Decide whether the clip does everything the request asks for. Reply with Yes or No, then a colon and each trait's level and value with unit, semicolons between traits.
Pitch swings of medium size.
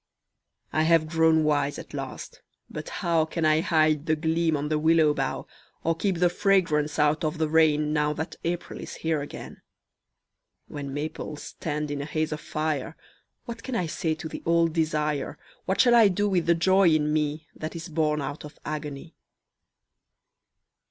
No: narrow, 1.7 semitones